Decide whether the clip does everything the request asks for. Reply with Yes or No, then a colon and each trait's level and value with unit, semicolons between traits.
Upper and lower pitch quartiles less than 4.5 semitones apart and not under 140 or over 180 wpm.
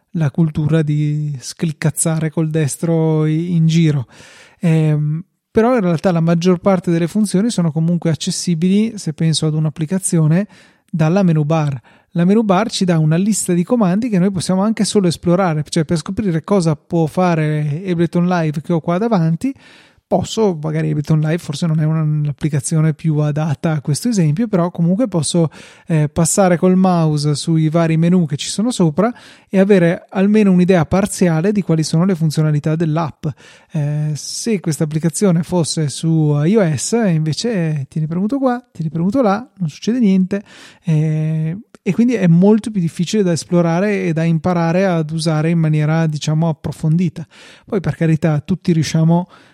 Yes: average, 3.1 semitones; average, 160 wpm